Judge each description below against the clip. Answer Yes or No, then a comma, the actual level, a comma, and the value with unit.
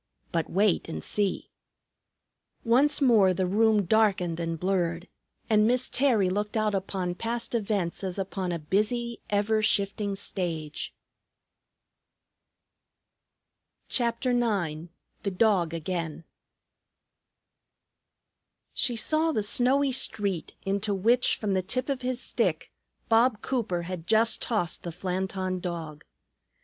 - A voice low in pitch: No, high, 200 Hz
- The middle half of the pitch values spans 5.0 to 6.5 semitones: No, average, 4.3 semitones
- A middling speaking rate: No, slow, 115 wpm